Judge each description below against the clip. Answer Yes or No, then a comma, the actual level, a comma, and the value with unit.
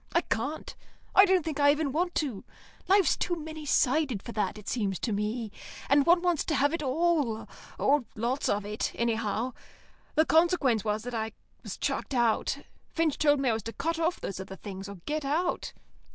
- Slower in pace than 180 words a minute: No, average, 195 wpm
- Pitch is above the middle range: Yes, very high, 275 Hz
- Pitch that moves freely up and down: Yes, wide, 6.4 semitones